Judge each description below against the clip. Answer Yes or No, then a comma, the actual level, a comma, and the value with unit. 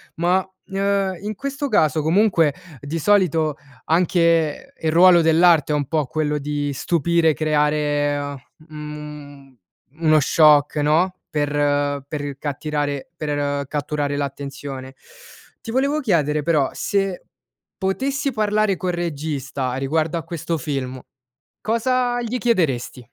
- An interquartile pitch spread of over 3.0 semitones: Yes, average, 4.1 semitones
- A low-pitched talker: No, medium, 155 Hz